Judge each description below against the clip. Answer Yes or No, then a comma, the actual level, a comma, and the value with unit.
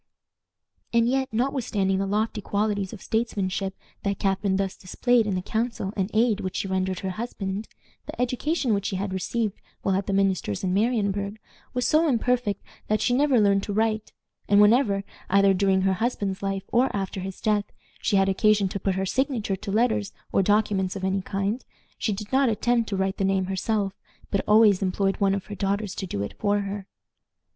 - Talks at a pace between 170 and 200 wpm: Yes, average, 195 wpm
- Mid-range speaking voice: No, high, 200 Hz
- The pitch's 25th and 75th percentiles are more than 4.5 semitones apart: No, narrow, 2.4 semitones